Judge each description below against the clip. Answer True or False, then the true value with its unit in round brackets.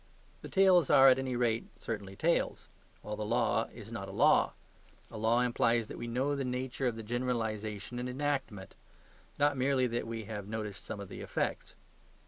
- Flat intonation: False (3.0 semitones)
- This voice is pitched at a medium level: False (120 Hz)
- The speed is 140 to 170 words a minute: False (185 wpm)